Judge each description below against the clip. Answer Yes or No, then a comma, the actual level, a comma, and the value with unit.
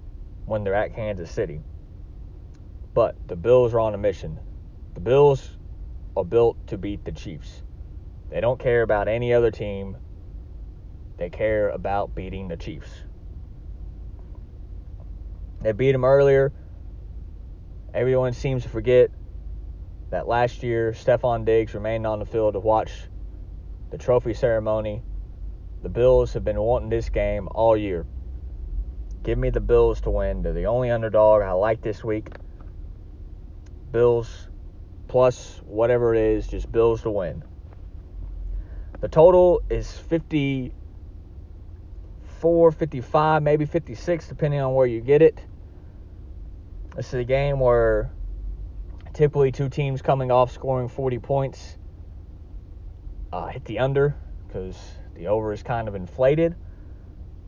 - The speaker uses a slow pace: Yes, slow, 130 wpm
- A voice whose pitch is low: Yes, very low, 95 Hz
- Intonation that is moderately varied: No, wide, 5.8 semitones